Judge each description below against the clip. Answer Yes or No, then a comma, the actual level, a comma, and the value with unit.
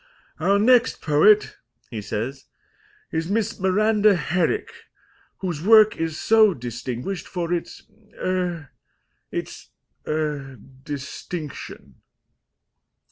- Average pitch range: No, wide, 6.1 semitones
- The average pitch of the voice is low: No, medium, 175 Hz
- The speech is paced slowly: Yes, slow, 90 wpm